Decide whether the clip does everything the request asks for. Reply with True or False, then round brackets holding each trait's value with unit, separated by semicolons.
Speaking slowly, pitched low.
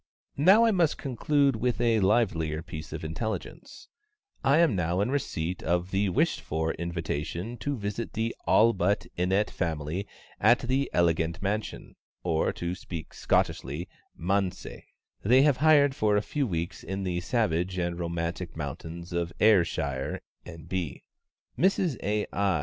False (145 wpm; 95 Hz)